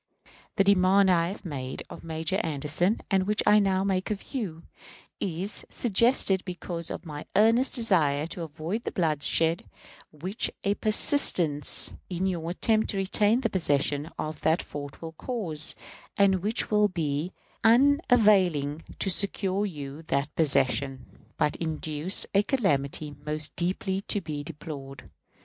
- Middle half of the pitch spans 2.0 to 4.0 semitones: No, average, 4.8 semitones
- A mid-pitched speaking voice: Yes, medium, 175 Hz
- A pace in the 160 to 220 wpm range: No, average, 140 wpm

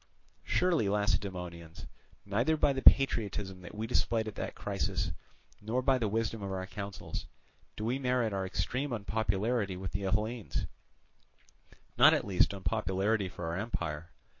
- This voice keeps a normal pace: Yes, average, 145 wpm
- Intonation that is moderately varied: Yes, average, 3.4 semitones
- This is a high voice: No, low, 105 Hz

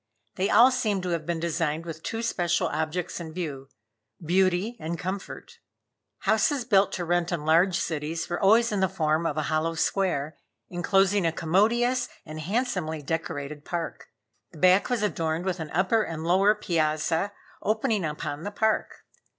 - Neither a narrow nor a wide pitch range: Yes, average, 3.9 semitones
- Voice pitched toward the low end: No, medium, 175 Hz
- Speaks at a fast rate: No, average, 165 wpm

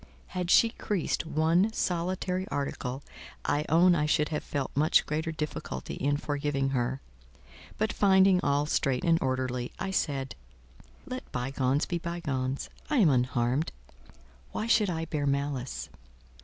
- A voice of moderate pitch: Yes, medium, 150 Hz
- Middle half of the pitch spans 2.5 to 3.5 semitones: No, average, 4.6 semitones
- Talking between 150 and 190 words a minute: No, average, 140 wpm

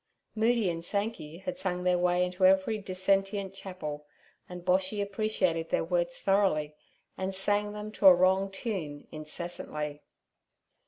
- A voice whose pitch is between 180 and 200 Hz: Yes, medium, 185 Hz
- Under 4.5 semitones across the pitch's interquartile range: Yes, narrow, 2.6 semitones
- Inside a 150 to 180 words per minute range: No, average, 140 wpm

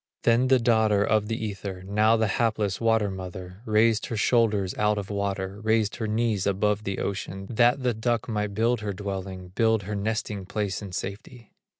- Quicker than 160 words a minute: Yes, average, 185 wpm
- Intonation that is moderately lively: No, narrow, 2.3 semitones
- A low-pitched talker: Yes, low, 105 Hz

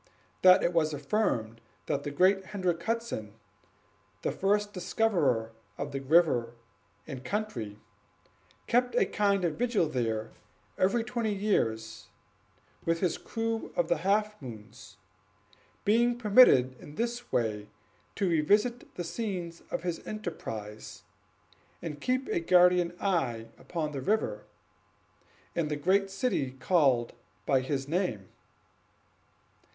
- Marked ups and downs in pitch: Yes, wide, 8.0 semitones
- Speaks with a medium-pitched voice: Yes, medium, 170 Hz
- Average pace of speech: No, slow, 125 wpm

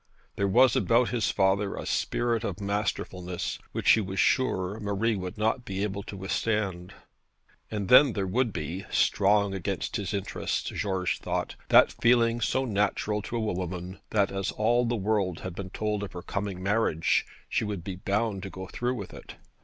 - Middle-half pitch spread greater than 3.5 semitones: No, average, 2.8 semitones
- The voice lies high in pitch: No, low, 100 Hz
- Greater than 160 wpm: Yes, average, 180 wpm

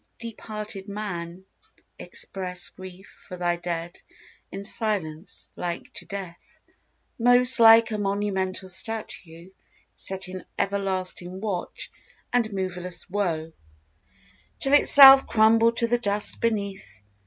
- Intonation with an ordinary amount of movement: Yes, average, 3.4 semitones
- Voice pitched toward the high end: Yes, high, 195 Hz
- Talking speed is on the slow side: Yes, slow, 110 wpm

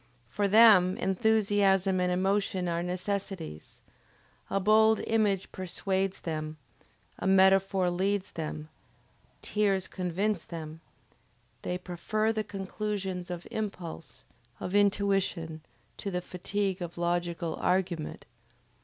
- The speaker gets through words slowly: Yes, slow, 105 wpm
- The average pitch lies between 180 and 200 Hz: Yes, high, 190 Hz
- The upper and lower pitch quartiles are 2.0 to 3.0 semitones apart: Yes, narrow, 2.4 semitones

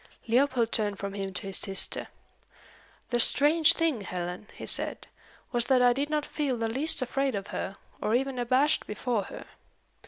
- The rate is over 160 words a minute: Yes, average, 175 wpm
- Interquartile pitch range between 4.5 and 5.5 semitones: Yes, average, 5.1 semitones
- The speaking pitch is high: Yes, high, 240 Hz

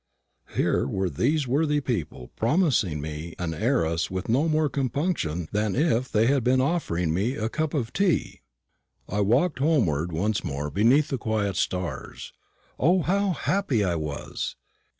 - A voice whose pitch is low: Yes, low, 115 Hz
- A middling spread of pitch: No, wide, 8.9 semitones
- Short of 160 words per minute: Yes, average, 150 wpm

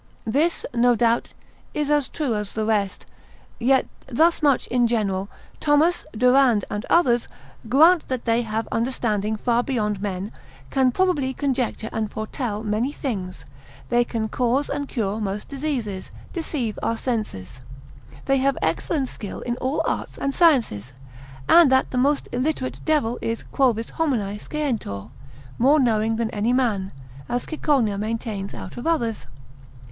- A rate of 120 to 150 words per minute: Yes, average, 145 wpm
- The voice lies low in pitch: No, high, 240 Hz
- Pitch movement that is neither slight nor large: Yes, average, 4.3 semitones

